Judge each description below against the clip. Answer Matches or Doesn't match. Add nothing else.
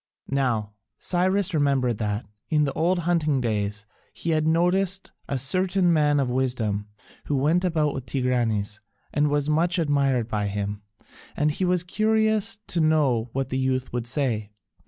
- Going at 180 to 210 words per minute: Doesn't match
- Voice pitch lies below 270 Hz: Matches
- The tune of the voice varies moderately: Doesn't match